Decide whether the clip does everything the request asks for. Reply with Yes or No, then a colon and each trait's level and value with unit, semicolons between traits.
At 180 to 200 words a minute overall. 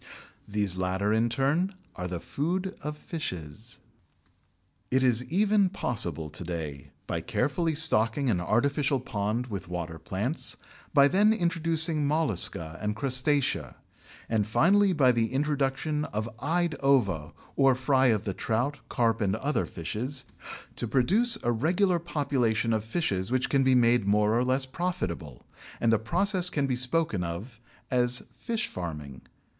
No: average, 145 wpm